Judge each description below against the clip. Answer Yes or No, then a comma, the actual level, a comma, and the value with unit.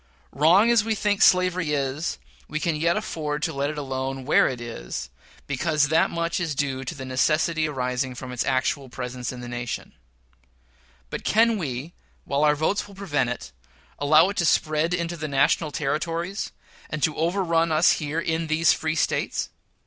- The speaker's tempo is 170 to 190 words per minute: Yes, average, 180 wpm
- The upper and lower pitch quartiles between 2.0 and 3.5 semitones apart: No, average, 3.9 semitones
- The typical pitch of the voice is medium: Yes, medium, 155 Hz